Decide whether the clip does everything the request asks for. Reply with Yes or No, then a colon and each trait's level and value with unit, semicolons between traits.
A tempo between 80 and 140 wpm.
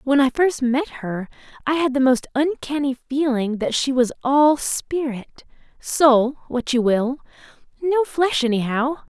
Yes: slow, 135 wpm